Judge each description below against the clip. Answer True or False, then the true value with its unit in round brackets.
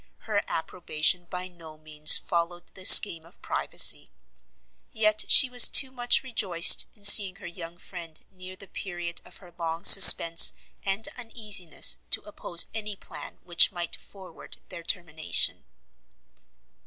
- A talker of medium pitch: True (180 Hz)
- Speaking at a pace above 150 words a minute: False (140 wpm)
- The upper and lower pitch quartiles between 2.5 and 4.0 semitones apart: True (3.3 semitones)